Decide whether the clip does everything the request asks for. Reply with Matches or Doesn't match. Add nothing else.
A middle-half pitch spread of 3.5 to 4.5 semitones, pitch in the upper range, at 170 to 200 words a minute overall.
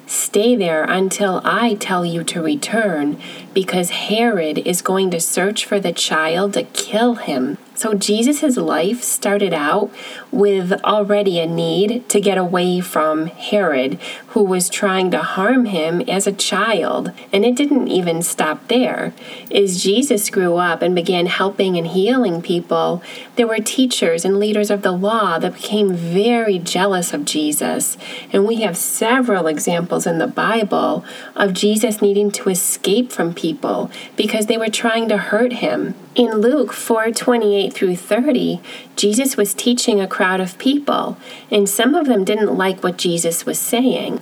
Doesn't match